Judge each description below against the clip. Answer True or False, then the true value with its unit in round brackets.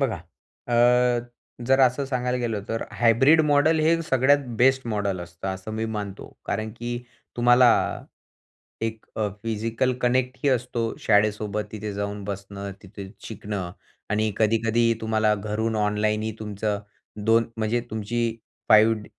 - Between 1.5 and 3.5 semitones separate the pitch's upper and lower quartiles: True (2.7 semitones)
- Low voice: True (110 Hz)